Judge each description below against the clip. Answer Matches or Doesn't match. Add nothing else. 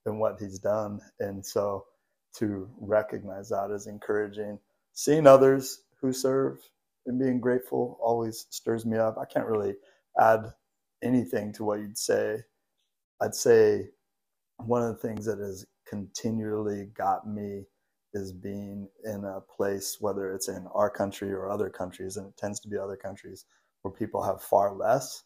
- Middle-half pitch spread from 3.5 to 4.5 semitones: Doesn't match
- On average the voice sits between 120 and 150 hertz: Doesn't match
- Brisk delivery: Doesn't match